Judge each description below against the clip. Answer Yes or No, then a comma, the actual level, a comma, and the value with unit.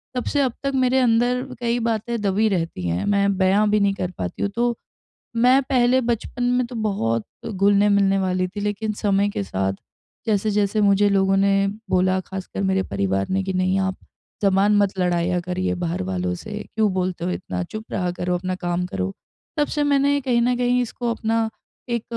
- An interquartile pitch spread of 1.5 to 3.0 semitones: No, average, 3.9 semitones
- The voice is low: No, high, 200 Hz